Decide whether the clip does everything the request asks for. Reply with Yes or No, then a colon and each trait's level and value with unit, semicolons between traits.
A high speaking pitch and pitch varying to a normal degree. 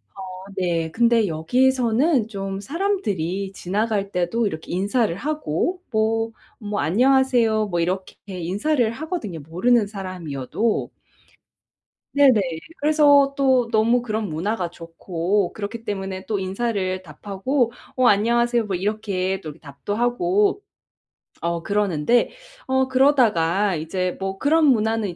Yes: high, 210 Hz; average, 4.8 semitones